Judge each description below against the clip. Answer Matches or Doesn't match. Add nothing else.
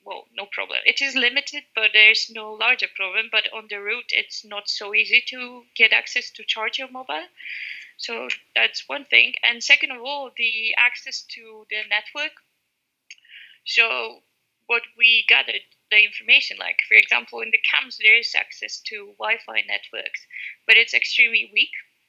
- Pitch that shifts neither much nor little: Matches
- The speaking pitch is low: Doesn't match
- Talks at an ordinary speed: Matches